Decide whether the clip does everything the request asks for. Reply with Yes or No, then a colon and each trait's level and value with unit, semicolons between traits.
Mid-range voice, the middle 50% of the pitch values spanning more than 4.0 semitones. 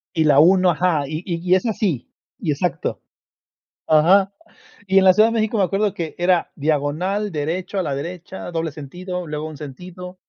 No: medium, 175 Hz; average, 3.4 semitones